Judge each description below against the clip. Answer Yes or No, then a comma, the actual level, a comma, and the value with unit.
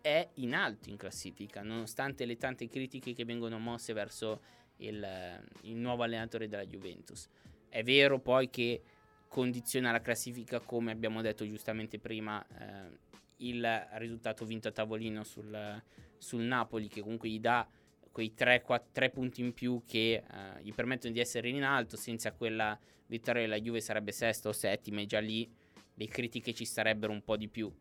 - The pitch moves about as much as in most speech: No, narrow, 2.0 semitones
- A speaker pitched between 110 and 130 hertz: Yes, low, 115 Hz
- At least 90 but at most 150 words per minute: No, average, 165 wpm